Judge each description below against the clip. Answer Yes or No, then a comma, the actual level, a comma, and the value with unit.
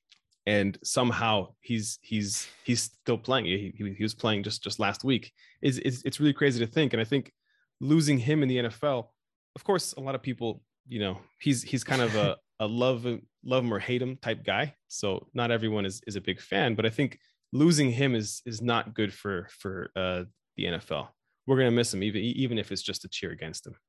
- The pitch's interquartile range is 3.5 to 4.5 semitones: Yes, average, 3.9 semitones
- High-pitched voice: No, low, 120 Hz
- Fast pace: Yes, fast, 225 wpm